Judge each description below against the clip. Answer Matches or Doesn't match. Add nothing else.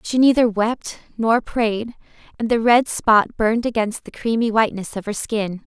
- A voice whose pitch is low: Doesn't match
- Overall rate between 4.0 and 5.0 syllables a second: Matches